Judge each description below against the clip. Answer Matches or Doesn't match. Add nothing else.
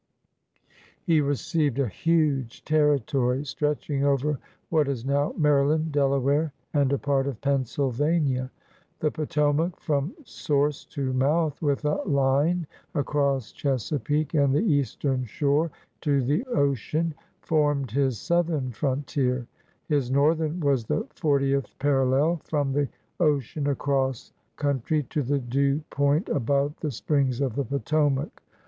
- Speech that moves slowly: Matches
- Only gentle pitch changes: Matches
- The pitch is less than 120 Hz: Doesn't match